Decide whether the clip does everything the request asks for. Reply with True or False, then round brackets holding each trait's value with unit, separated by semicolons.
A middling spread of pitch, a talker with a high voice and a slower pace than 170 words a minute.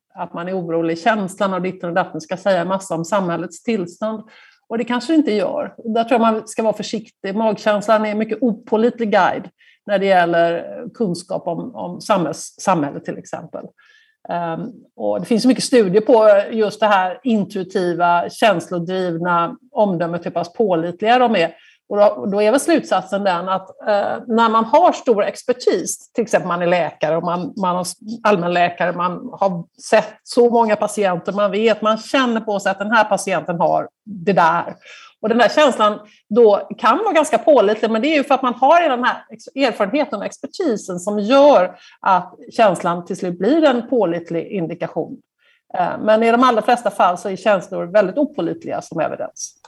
False (4.4 semitones; 210 Hz; 175 wpm)